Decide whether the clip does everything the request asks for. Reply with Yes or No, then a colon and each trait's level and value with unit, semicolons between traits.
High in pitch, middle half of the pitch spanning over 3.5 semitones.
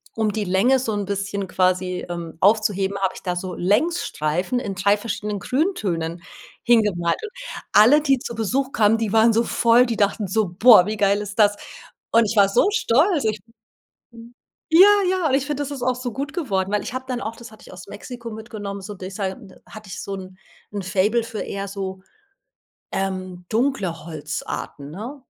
Yes: high, 210 Hz; average, 4.1 semitones